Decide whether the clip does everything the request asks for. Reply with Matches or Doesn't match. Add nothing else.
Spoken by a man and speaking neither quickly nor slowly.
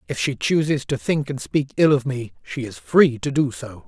Doesn't match